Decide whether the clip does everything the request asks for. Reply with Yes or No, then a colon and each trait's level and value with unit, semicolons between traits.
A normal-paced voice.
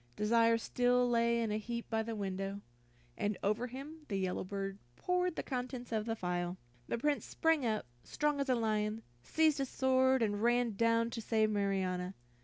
Yes: average, 185 wpm